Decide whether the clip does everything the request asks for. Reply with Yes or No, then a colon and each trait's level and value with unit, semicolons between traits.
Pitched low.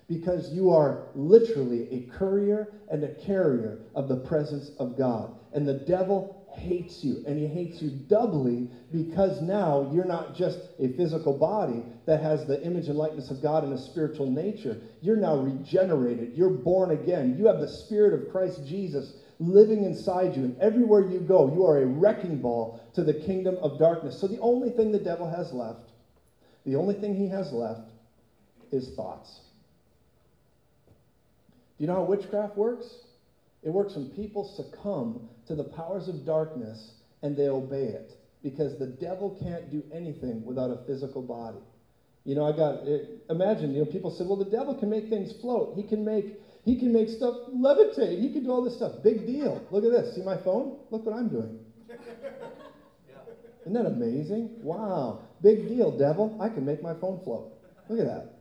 No: medium, 175 Hz